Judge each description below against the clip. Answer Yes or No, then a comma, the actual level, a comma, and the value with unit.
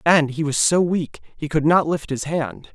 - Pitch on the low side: No, medium, 155 Hz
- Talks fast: Yes, fast, 240 wpm